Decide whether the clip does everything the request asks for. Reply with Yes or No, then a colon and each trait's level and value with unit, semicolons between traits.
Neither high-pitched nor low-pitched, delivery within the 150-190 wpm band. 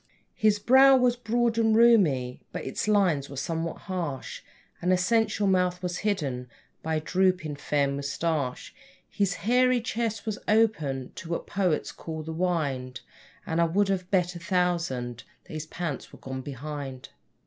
Yes: medium, 180 Hz; average, 160 wpm